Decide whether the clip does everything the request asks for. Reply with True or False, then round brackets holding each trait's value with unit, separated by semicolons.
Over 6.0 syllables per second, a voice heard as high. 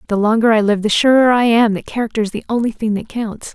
True (6.4 syllables/s; 220 Hz)